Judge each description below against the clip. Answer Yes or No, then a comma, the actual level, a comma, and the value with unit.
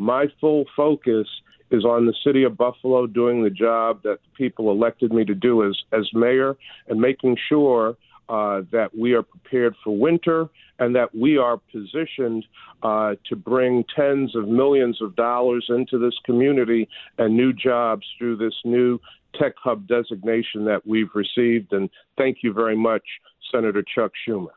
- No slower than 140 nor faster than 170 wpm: Yes, average, 165 wpm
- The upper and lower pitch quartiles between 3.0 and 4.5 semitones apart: No, narrow, 2.4 semitones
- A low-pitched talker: Yes, low, 120 Hz